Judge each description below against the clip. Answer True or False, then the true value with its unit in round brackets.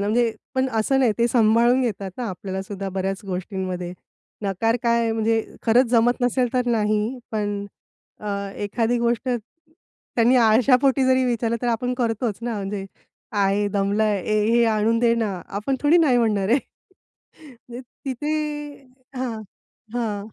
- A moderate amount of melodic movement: True (3.1 semitones)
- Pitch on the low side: False (230 Hz)